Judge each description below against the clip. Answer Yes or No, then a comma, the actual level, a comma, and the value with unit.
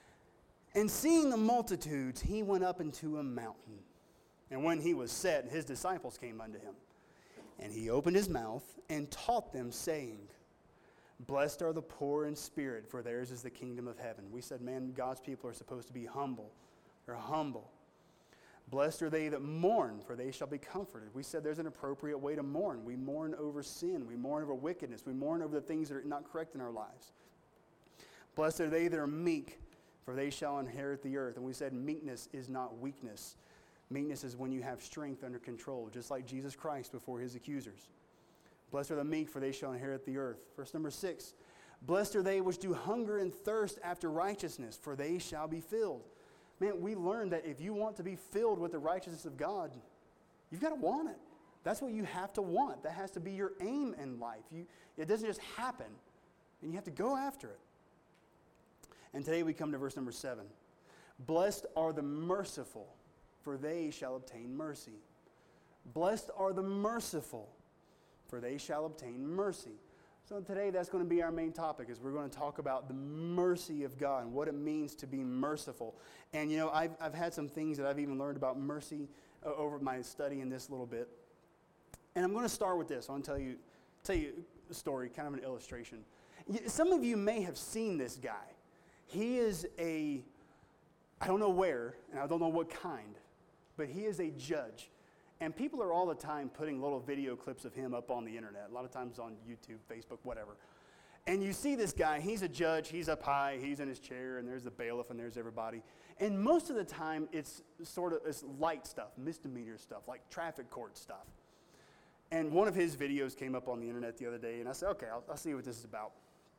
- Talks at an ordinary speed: No, fast, 210 wpm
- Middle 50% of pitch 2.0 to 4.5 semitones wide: No, average, 5.2 semitones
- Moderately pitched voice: Yes, medium, 150 Hz